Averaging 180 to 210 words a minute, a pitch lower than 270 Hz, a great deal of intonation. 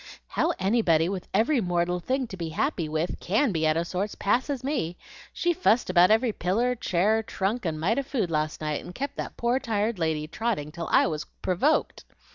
Yes: average, 200 wpm; high, 190 Hz; wide, 6.1 semitones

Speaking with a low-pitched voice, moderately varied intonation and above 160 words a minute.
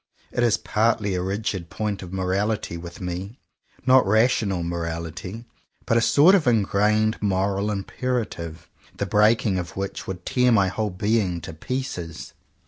No: low, 100 Hz; average, 3.8 semitones; average, 150 wpm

